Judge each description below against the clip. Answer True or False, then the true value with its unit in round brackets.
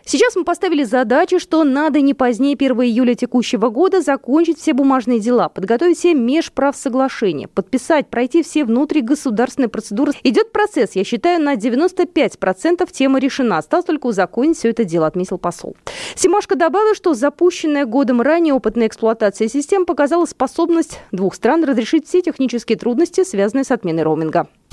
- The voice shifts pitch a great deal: True (5.7 semitones)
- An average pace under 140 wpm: False (150 wpm)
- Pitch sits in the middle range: False (275 Hz)